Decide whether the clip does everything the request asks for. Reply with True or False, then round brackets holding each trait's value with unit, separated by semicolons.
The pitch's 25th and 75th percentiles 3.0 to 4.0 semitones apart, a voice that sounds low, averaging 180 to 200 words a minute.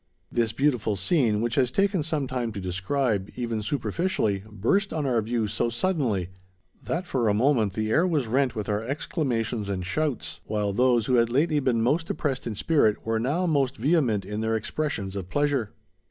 False (5.1 semitones; 120 Hz; 185 wpm)